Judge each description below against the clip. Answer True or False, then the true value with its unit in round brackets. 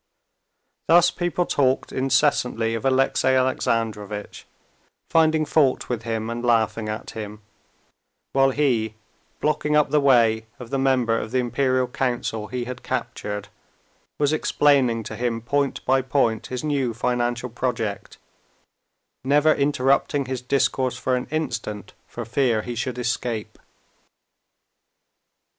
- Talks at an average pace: False (125 wpm)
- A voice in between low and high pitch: False (125 Hz)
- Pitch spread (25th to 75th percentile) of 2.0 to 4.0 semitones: True (3.1 semitones)